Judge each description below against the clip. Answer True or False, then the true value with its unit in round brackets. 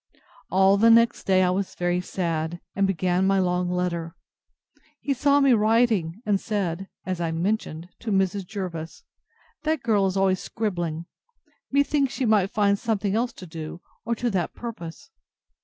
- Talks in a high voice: True (195 Hz)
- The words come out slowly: False (160 wpm)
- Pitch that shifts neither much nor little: True (4.0 semitones)